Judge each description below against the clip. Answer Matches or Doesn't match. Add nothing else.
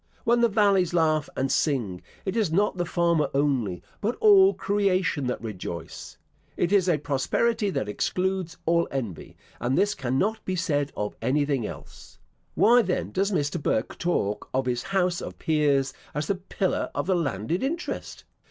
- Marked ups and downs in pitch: Matches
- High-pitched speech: Doesn't match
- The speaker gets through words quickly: Doesn't match